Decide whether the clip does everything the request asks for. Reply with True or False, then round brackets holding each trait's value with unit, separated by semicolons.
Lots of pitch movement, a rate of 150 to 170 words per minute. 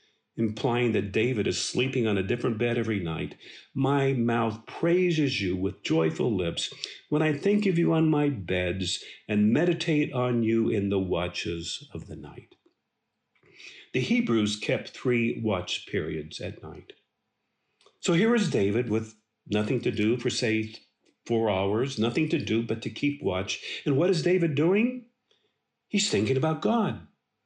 True (6.7 semitones; 155 wpm)